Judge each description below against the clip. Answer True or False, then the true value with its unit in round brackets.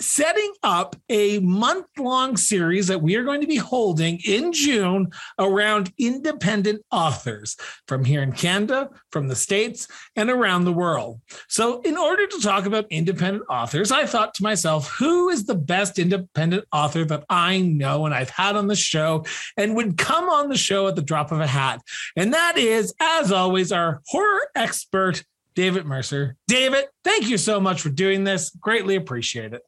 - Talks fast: False (180 wpm)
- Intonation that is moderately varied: False (6.2 semitones)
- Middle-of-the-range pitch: False (195 Hz)